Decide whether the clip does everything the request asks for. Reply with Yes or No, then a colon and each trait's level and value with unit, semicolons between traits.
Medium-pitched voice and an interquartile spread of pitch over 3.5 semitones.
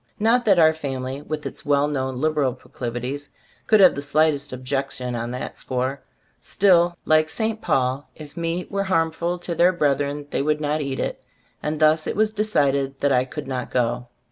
Yes: medium, 145 Hz; average, 3.9 semitones